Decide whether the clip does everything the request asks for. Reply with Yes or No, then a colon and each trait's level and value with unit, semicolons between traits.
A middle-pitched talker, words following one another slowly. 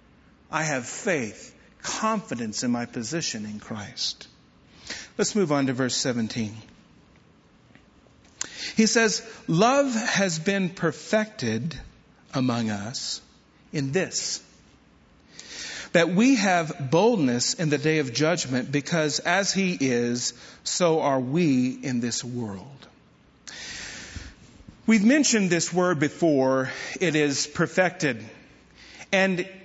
Yes: medium, 155 Hz; slow, 105 wpm